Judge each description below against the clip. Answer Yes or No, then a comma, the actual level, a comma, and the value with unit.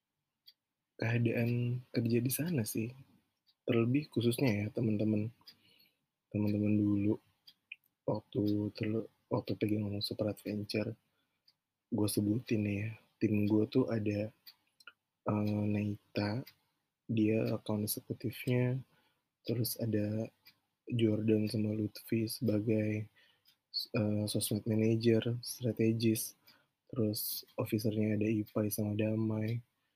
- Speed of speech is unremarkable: Yes, average, 95 wpm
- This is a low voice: Yes, low, 110 Hz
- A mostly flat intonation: Yes, narrow, 1.8 semitones